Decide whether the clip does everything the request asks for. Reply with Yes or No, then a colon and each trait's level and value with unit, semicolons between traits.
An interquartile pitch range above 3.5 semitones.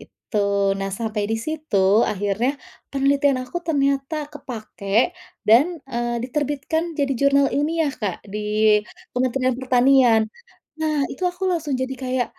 Yes: average, 4.9 semitones